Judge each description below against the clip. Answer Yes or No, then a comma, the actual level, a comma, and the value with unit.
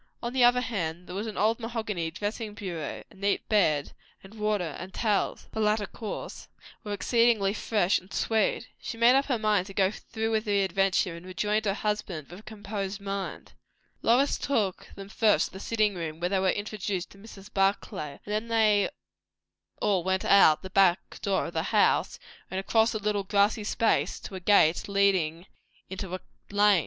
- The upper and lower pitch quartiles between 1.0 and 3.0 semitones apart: Yes, narrow, 2.4 semitones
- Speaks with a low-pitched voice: No, high, 200 Hz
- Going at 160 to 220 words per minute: Yes, average, 190 wpm